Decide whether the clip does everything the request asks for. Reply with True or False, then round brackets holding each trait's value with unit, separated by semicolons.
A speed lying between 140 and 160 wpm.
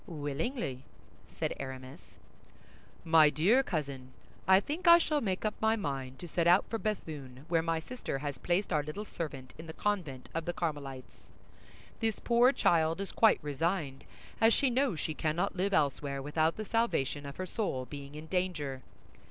False (170 wpm)